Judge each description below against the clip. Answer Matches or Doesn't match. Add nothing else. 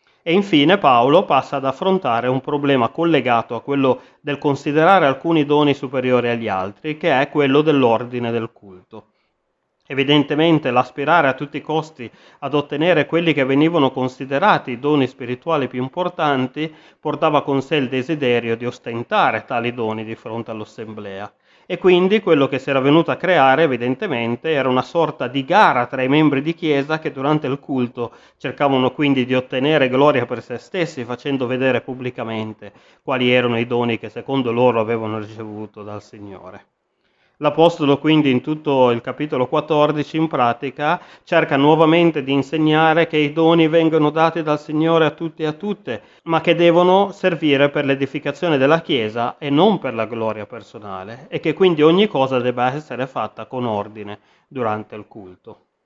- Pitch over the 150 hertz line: Doesn't match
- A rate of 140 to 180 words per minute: Matches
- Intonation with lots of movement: Doesn't match